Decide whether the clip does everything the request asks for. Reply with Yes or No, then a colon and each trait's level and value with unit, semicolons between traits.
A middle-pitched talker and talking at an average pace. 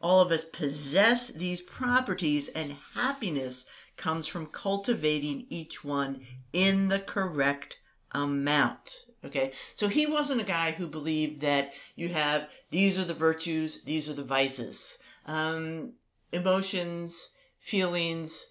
No: medium, 160 Hz; slow, 125 wpm